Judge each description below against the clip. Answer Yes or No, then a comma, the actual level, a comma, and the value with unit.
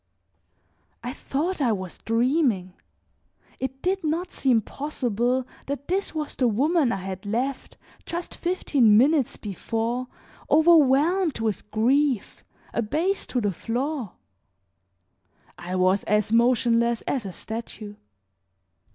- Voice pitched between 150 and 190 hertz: No, very high, 250 Hz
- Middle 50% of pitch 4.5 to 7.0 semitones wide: Yes, average, 5.2 semitones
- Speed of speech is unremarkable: No, slow, 115 wpm